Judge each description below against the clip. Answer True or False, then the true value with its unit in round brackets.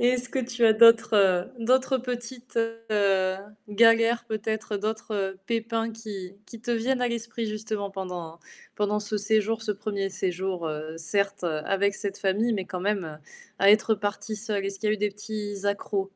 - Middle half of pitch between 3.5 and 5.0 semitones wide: False (2.7 semitones)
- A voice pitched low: False (210 Hz)